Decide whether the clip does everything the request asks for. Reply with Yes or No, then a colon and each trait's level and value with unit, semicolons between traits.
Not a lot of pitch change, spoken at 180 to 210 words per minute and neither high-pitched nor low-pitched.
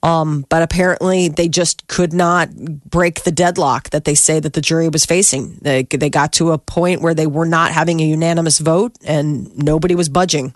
Yes: narrow, 2.3 semitones; fast, 205 wpm; medium, 165 Hz